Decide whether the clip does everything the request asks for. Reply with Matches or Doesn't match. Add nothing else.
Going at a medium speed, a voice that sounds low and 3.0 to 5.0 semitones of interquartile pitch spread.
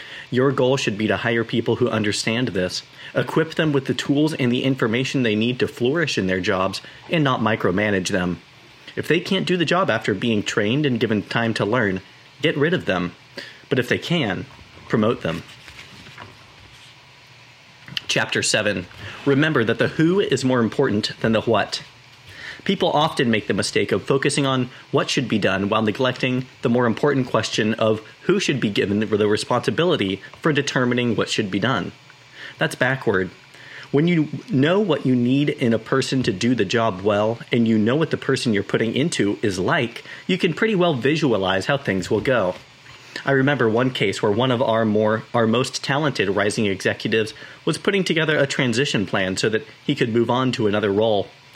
Matches